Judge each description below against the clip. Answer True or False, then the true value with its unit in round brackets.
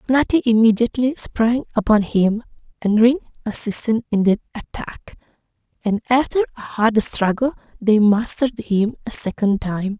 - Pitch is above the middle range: True (225 Hz)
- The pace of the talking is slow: True (130 wpm)